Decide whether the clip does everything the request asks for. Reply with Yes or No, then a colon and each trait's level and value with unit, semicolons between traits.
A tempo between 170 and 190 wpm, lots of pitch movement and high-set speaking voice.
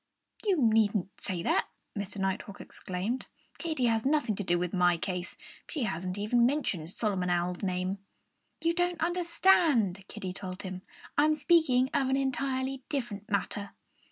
No: average, 155 wpm; wide, 6.7 semitones; high, 215 Hz